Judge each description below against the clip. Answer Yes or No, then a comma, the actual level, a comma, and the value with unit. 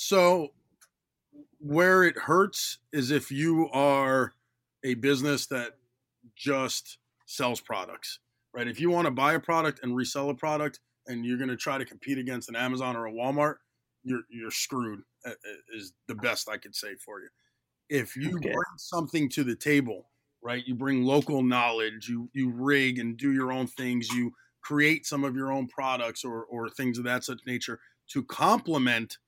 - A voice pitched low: Yes, low, 130 Hz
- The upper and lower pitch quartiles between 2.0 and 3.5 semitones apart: Yes, average, 2.9 semitones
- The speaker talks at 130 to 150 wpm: No, average, 175 wpm